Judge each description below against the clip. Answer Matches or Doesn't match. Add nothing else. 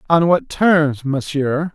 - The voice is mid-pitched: Matches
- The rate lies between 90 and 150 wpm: Matches